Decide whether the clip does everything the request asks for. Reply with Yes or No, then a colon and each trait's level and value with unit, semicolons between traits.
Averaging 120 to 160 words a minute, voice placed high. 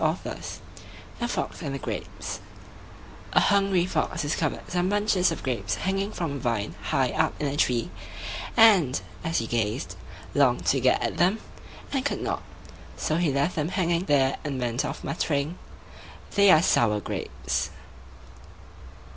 No: average, 145 wpm; medium, 150 Hz